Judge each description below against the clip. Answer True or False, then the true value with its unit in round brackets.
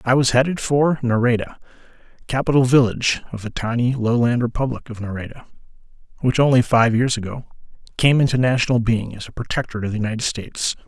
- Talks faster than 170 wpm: False (165 wpm)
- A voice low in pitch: True (120 Hz)